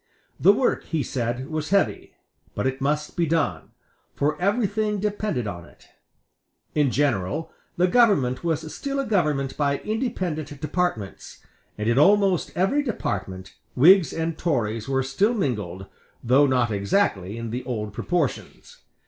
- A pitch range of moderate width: No, wide, 7.6 semitones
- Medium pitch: Yes, medium, 150 Hz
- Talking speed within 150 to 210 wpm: No, average, 140 wpm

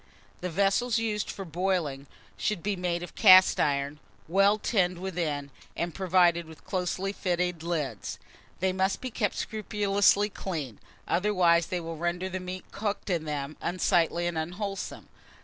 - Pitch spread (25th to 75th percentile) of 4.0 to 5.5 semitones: No, average, 2.8 semitones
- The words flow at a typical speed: Yes, average, 150 wpm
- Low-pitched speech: No, medium, 180 Hz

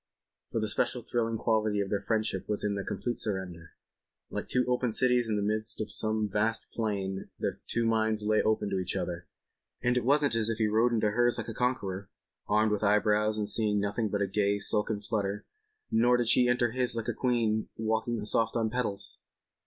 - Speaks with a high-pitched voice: No, low, 110 Hz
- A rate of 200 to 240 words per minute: Yes, fast, 205 wpm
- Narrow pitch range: Yes, narrow, 2.2 semitones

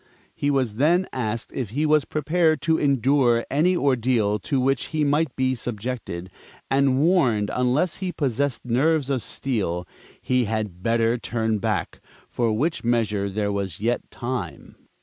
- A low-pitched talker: Yes, low, 125 Hz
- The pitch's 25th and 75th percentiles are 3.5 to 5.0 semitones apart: Yes, average, 4.4 semitones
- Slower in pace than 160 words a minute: Yes, average, 150 wpm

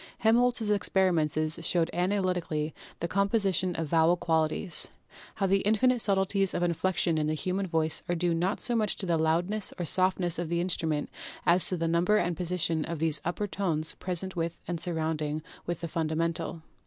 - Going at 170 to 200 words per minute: Yes, average, 185 wpm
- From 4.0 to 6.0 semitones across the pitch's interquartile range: No, average, 2.9 semitones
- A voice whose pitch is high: No, medium, 175 Hz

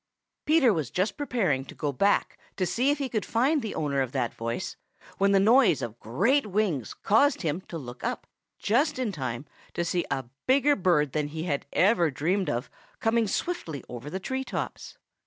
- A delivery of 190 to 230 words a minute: Yes, average, 195 wpm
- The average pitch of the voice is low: No, medium, 185 Hz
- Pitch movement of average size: No, wide, 8.6 semitones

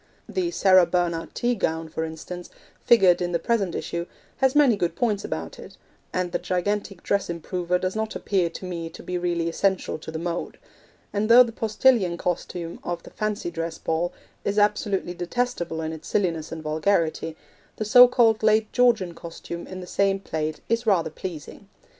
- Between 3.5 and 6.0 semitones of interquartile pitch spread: Yes, average, 4.0 semitones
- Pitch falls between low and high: Yes, medium, 180 Hz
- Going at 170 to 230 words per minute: Yes, average, 180 wpm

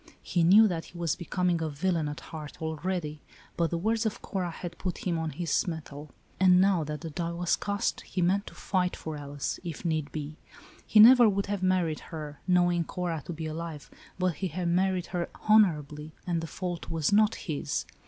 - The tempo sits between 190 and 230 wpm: Yes, average, 200 wpm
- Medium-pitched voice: Yes, medium, 170 Hz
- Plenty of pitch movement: No, average, 2.9 semitones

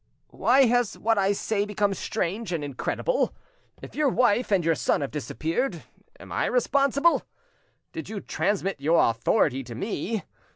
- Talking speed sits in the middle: Yes, average, 155 wpm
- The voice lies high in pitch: Yes, high, 205 Hz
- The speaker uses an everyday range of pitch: No, wide, 6.7 semitones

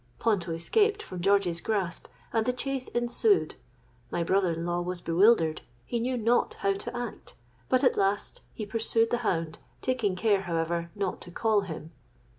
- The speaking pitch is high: Yes, high, 200 Hz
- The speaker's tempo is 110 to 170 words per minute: Yes, average, 165 wpm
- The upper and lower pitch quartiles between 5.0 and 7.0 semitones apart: Yes, average, 5.3 semitones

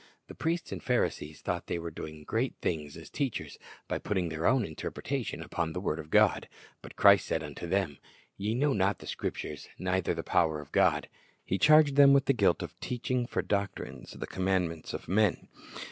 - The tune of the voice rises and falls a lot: Yes, wide, 7.0 semitones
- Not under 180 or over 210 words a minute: Yes, average, 195 wpm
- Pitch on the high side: No, very low, 95 Hz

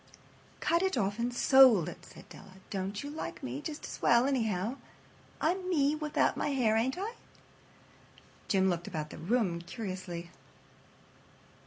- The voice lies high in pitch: Yes, high, 230 Hz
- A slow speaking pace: No, average, 150 wpm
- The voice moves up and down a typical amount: No, wide, 7.1 semitones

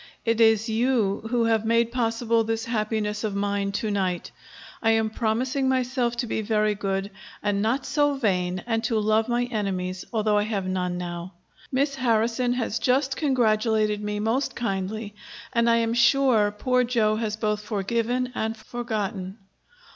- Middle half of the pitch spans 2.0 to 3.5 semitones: Yes, narrow, 2.5 semitones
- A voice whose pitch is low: No, high, 220 Hz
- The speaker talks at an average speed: Yes, average, 160 wpm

